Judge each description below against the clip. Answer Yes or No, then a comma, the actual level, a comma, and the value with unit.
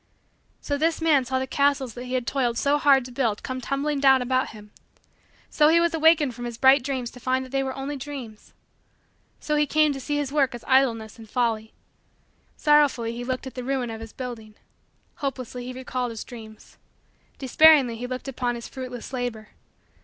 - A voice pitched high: Yes, very high, 260 Hz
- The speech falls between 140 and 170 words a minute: No, average, 200 wpm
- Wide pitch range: No, narrow, 2.6 semitones